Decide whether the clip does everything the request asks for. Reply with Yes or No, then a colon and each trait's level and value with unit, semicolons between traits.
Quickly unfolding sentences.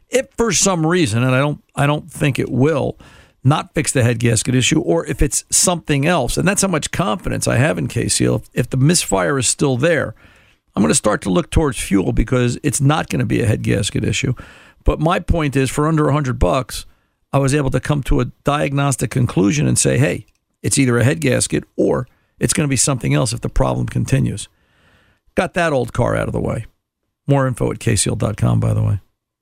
Yes: fast, 215 wpm